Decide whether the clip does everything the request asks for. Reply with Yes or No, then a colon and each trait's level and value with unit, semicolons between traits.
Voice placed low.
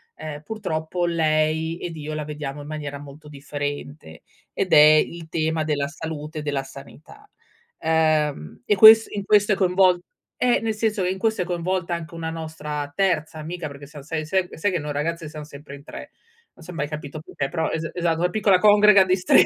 No: medium, 160 Hz